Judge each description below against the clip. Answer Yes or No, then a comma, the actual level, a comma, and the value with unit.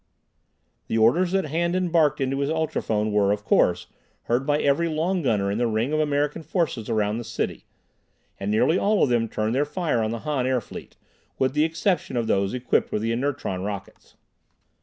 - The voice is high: No, low, 130 Hz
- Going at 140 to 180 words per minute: No, average, 190 wpm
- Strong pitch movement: Yes, wide, 6.4 semitones